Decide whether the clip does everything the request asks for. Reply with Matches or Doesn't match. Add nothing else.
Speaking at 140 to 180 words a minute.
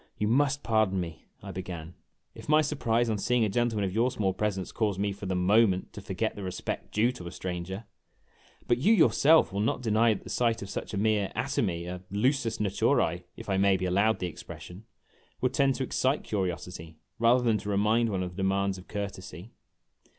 Doesn't match